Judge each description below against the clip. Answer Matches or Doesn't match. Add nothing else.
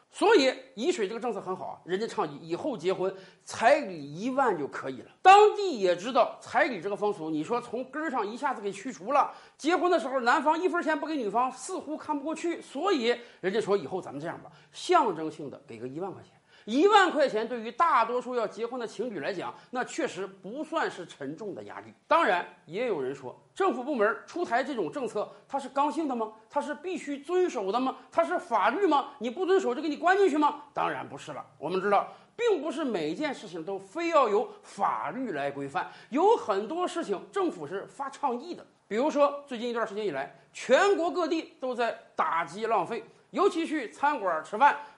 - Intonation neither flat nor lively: Doesn't match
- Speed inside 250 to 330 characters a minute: Matches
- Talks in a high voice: Matches